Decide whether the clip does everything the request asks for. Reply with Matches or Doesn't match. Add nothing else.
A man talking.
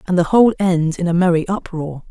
Doesn't match